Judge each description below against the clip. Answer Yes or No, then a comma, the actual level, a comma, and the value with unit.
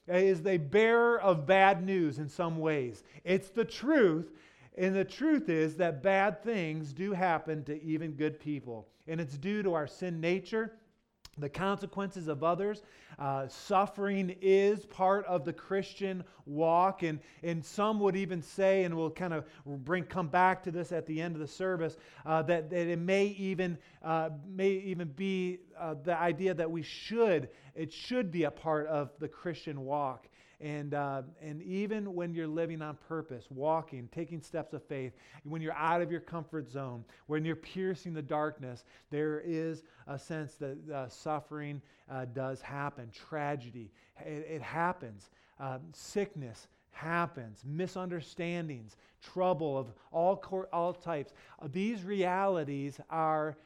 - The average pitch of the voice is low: No, medium, 165 Hz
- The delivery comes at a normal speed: Yes, average, 160 wpm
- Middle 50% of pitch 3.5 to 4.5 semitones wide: Yes, average, 3.9 semitones